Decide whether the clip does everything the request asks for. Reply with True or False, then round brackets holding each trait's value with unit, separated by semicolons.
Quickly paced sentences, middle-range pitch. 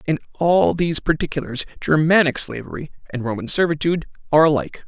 False (135 wpm; 150 Hz)